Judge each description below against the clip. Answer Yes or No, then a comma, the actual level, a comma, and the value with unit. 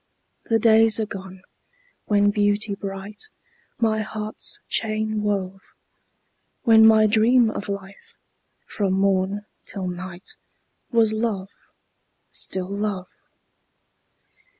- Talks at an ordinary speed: No, slow, 100 wpm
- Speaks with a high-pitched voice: Yes, high, 205 Hz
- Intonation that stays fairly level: Yes, narrow, 2.0 semitones